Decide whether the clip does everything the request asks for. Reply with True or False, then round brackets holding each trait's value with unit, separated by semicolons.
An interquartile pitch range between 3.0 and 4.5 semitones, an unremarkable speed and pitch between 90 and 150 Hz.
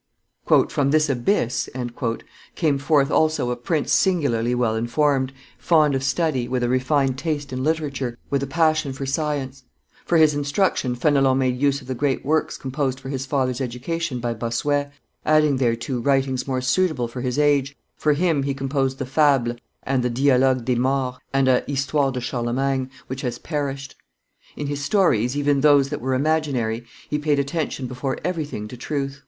False (2.5 semitones; 175 wpm; 135 Hz)